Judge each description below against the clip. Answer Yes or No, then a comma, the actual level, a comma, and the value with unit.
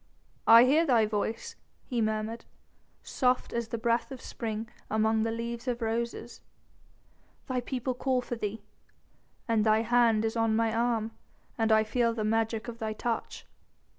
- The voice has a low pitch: No, high, 230 Hz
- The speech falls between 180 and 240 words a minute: No, average, 160 wpm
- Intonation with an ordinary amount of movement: No, narrow, 1.5 semitones